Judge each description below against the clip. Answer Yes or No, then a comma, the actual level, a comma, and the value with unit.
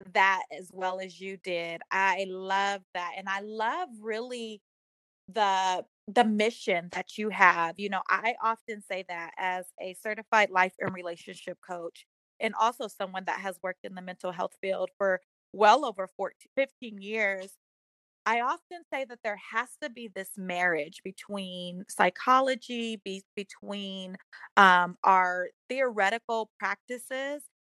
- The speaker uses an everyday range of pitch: Yes, average, 3.2 semitones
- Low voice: No, high, 195 Hz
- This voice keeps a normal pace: Yes, average, 145 wpm